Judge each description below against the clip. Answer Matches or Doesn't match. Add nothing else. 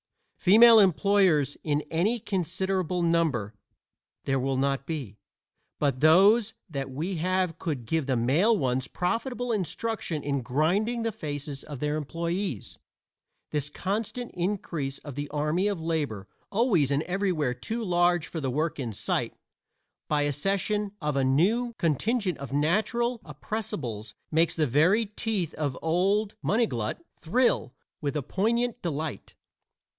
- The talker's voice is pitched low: Doesn't match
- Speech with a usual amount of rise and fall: Doesn't match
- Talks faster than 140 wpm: Doesn't match